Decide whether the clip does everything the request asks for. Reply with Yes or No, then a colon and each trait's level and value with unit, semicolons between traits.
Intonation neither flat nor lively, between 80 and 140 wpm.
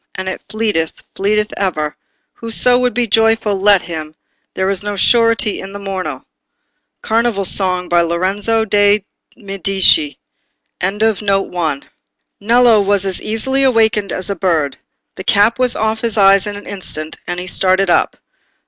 Yes: average, 3.0 semitones; slow, 135 wpm